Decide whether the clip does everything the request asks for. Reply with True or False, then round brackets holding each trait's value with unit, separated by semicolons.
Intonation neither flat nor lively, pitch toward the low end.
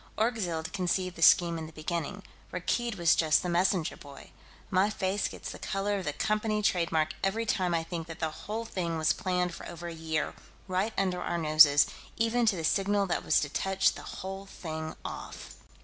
False (3.3 semitones; 180 Hz)